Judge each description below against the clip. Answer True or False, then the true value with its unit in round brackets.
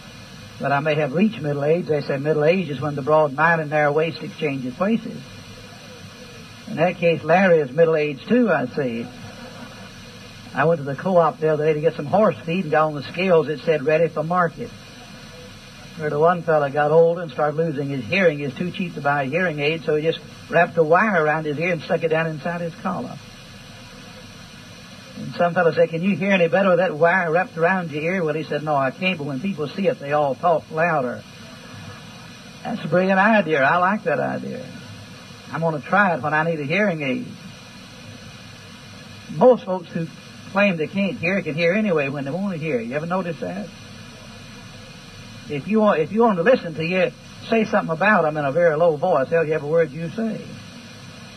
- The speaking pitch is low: False (165 Hz)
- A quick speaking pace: True (215 wpm)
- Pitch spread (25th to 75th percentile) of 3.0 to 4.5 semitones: True (3.4 semitones)